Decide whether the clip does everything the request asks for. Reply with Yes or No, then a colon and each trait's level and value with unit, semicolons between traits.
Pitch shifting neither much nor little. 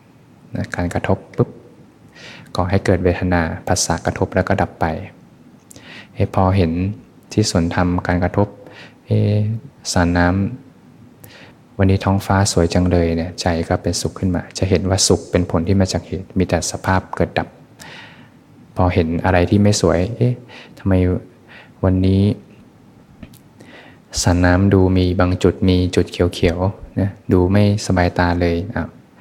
No: narrow, 2.1 semitones